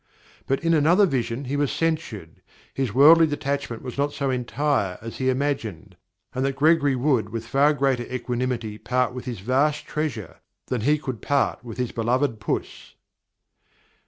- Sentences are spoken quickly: No, average, 160 wpm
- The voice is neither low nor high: No, low, 130 Hz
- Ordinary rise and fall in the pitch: Yes, average, 3.4 semitones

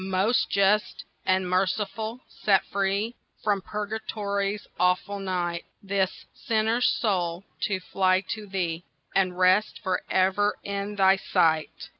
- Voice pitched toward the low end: No, high, 195 Hz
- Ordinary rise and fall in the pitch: No, narrow, 2.0 semitones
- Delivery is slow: Yes, slow, 120 wpm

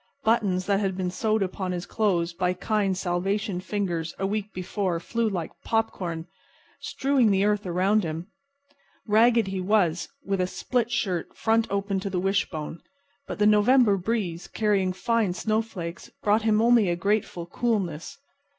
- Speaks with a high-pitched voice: Yes, high, 195 Hz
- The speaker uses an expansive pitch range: No, average, 3.2 semitones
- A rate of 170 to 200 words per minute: No, average, 155 wpm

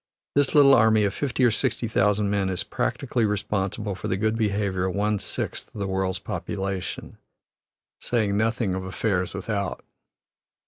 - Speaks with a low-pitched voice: Yes, low, 105 Hz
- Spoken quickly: No, average, 155 wpm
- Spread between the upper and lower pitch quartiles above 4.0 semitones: No, narrow, 2.6 semitones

